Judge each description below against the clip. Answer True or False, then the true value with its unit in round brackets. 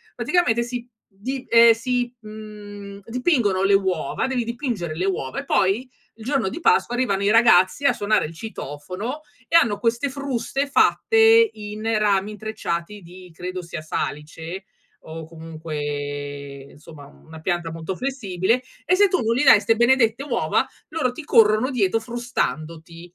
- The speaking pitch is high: True (210 Hz)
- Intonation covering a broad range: True (6.4 semitones)